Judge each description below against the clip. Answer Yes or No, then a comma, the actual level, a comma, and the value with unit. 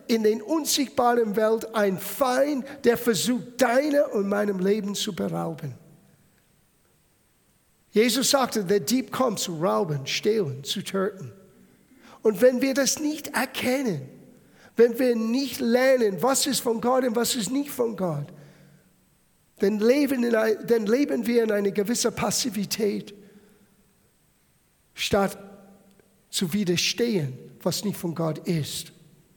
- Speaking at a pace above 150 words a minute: No, average, 130 wpm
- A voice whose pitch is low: No, high, 215 Hz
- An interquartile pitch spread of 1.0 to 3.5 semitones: No, average, 4.2 semitones